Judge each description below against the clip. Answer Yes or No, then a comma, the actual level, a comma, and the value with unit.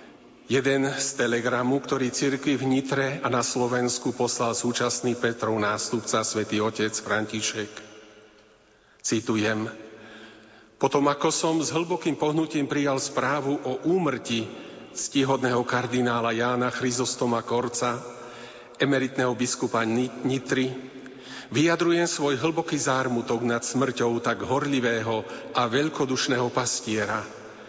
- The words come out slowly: Yes, slow, 100 wpm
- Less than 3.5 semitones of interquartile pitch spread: Yes, average, 2.9 semitones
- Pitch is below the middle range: Yes, low, 125 Hz